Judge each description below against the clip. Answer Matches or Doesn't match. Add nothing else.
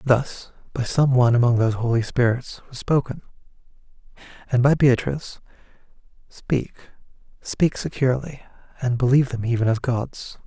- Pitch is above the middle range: Doesn't match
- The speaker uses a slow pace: Matches